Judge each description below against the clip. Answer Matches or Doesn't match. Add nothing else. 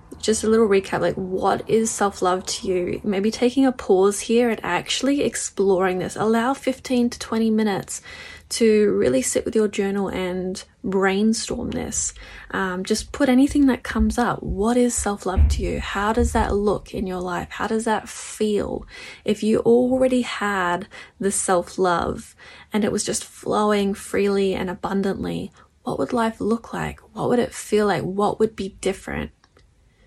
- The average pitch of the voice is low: Doesn't match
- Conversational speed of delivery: Matches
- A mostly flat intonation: Doesn't match